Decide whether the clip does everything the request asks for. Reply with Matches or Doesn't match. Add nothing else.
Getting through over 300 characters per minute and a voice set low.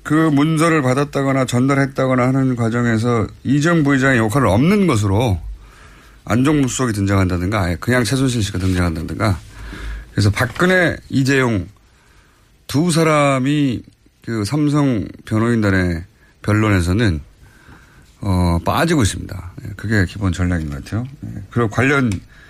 Doesn't match